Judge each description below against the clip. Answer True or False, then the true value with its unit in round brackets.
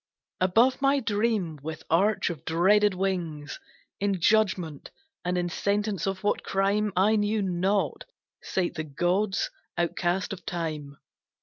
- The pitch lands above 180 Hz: True (190 Hz)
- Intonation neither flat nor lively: True (3.3 semitones)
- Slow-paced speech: True (130 wpm)